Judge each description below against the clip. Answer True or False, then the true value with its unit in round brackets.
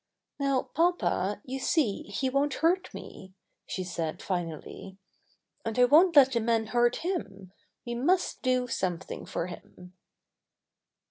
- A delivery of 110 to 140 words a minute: True (135 wpm)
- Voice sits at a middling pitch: False (240 Hz)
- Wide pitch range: True (6.7 semitones)